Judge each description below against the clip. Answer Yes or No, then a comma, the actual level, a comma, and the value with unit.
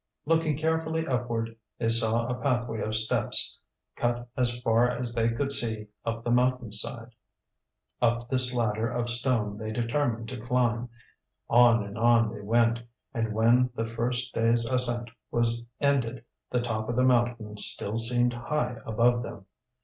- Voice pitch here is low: Yes, low, 120 Hz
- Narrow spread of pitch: Yes, narrow, 1.4 semitones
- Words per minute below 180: Yes, average, 155 wpm